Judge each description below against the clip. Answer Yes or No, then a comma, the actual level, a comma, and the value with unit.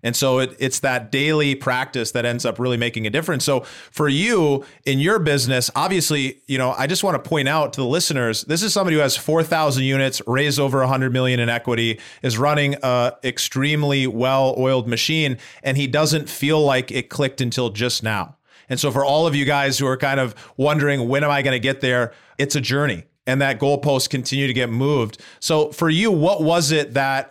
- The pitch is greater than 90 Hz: Yes, low, 135 Hz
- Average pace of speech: No, fast, 215 wpm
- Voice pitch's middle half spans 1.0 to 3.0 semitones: Yes, narrow, 2.4 semitones